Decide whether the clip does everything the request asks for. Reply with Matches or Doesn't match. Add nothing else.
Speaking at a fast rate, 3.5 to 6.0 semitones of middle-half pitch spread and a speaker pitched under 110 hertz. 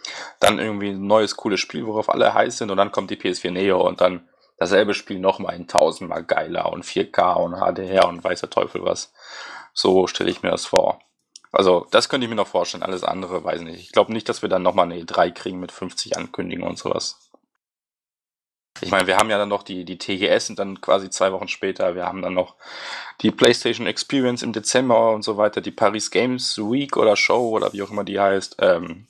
Doesn't match